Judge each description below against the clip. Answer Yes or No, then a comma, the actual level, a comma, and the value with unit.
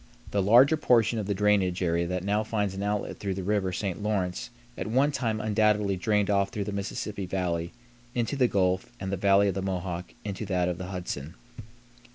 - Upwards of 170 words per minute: Yes, fast, 205 wpm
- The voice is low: Yes, low, 100 Hz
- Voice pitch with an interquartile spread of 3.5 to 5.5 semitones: No, narrow, 2.4 semitones